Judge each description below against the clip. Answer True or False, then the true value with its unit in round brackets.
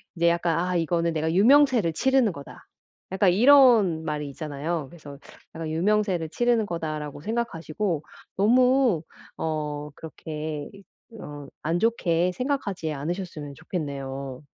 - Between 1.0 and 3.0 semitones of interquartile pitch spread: False (5.3 semitones)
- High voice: False (170 Hz)